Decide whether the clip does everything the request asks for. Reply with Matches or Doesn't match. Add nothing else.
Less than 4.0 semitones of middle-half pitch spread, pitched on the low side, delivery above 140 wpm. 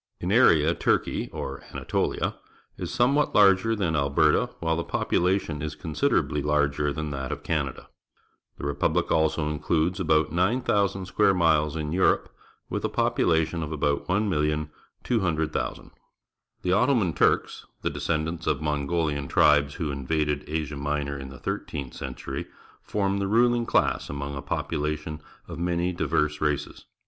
Doesn't match